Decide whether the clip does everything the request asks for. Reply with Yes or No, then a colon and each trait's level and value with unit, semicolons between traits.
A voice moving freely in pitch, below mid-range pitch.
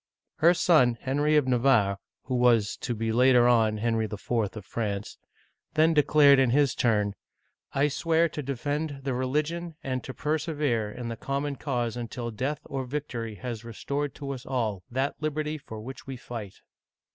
No: average, 4.0 semitones; low, 130 Hz